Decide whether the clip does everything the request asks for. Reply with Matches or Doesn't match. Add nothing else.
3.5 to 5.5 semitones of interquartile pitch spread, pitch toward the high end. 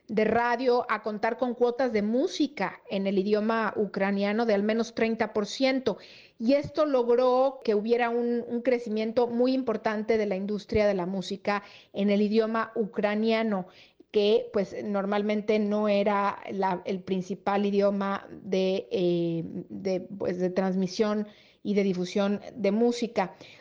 Doesn't match